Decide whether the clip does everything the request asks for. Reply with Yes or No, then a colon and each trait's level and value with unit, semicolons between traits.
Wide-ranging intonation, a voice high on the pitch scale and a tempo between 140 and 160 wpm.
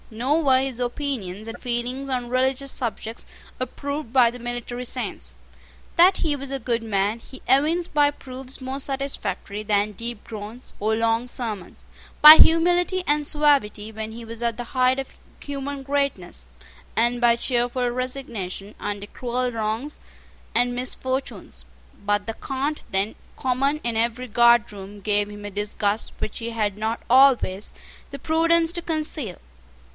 No: average, 3.9 semitones; high, 245 Hz; average, 150 wpm